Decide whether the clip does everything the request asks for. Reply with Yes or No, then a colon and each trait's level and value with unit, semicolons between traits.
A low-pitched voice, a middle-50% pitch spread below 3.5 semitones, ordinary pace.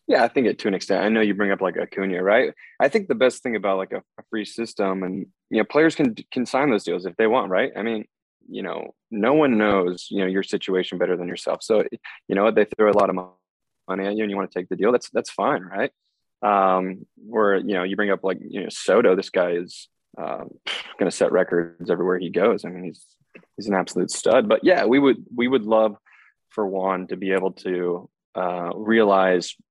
No: very low, 95 Hz; average, 2.9 semitones; fast, 235 wpm